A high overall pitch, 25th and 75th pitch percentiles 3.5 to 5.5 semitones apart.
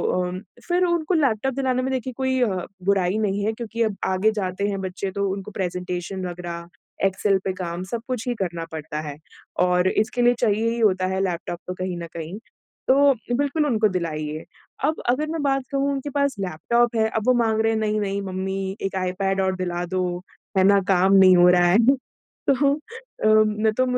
Yes: high, 200 Hz; average, 4.7 semitones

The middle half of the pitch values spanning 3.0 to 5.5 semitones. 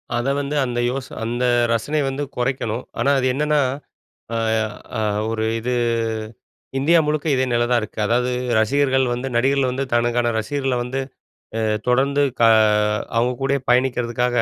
No: narrow, 2.4 semitones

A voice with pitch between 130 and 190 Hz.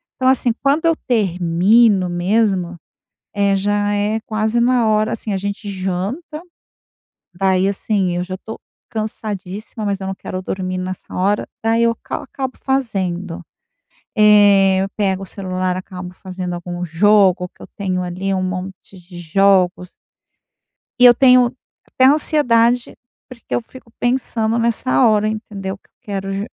No: high, 200 Hz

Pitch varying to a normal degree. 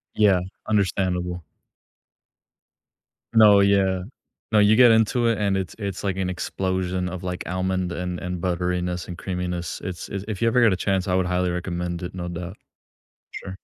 No: narrow, 1.9 semitones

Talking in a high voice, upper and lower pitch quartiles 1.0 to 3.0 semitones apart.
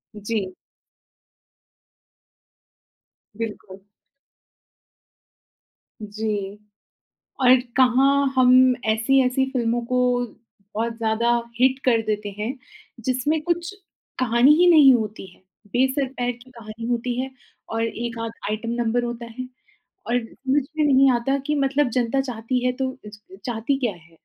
Yes: high, 245 Hz; average, 2.7 semitones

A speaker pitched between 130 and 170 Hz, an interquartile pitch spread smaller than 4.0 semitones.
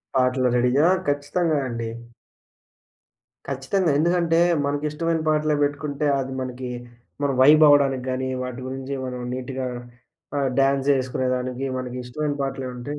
Yes: low, 135 Hz; narrow, 2.6 semitones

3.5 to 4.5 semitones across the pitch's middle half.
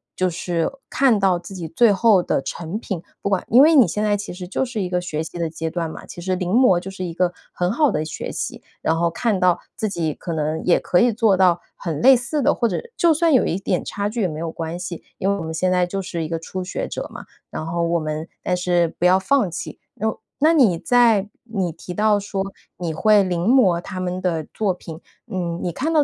Yes: average, 3.9 semitones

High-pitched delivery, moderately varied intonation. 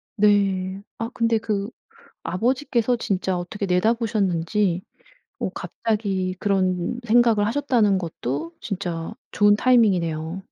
Yes: high, 200 Hz; average, 3.6 semitones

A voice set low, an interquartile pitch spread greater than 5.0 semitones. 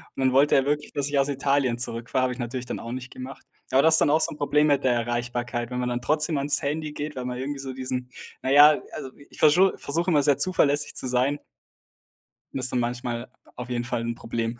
No: low, 130 Hz; average, 2.9 semitones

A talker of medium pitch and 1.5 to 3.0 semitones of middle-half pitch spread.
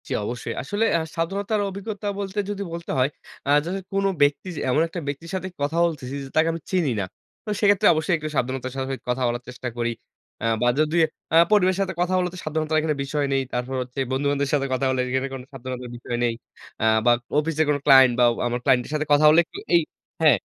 No: medium, 150 Hz; average, 5.2 semitones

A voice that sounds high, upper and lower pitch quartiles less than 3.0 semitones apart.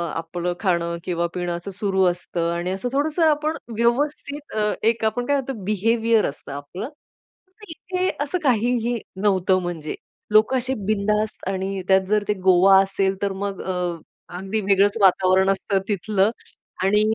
No: high, 200 Hz; average, 3.7 semitones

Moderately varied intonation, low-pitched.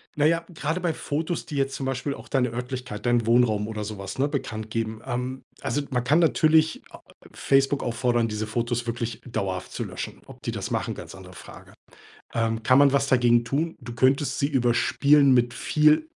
Yes: average, 3.5 semitones; low, 125 Hz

